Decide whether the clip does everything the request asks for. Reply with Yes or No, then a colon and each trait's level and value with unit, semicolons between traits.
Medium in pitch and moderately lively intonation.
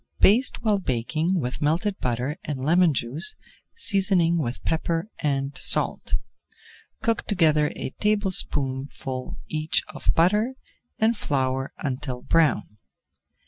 No: medium, 155 Hz; wide, 6.3 semitones